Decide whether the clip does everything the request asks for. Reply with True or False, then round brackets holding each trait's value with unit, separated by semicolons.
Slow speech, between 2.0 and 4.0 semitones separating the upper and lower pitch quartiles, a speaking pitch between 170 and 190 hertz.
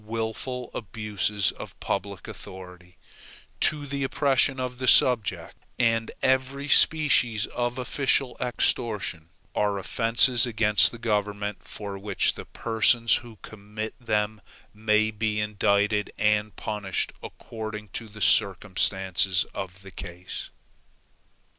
False (115 wpm; 2.9 semitones; 110 Hz)